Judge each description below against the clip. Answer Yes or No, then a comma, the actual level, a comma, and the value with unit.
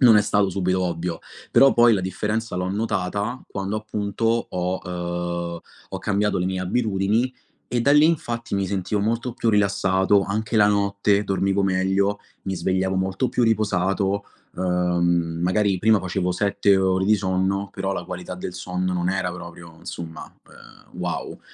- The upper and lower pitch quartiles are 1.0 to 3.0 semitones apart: Yes, narrow, 2.4 semitones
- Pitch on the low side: Yes, very low, 95 Hz